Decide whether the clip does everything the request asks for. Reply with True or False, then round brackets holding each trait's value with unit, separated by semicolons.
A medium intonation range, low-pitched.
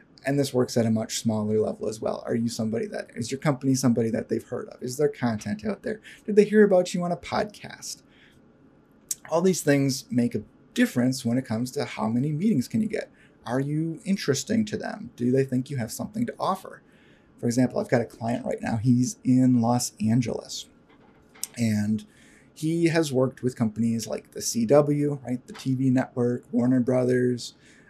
True (4.5 semitones; 130 Hz)